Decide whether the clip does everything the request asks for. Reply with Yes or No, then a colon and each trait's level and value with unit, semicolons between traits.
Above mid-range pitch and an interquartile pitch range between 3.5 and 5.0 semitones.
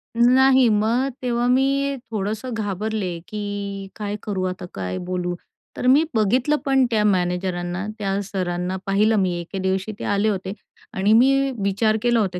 Yes: high, 205 Hz; average, 4.0 semitones